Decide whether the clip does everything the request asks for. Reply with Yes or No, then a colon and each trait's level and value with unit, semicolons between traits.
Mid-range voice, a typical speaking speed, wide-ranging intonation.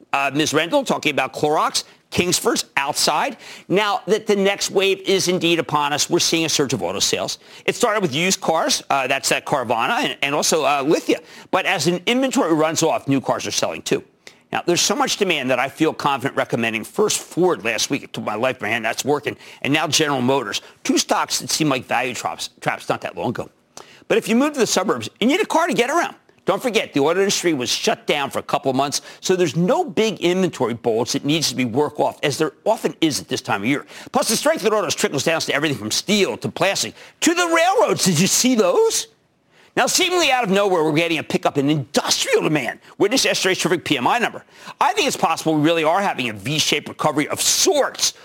No: medium, 170 Hz; fast, 230 wpm; wide, 6.1 semitones